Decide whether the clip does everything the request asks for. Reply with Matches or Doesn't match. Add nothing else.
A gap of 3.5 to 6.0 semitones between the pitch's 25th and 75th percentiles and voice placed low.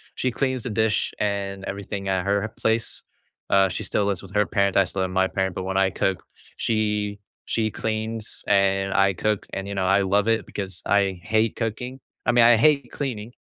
Doesn't match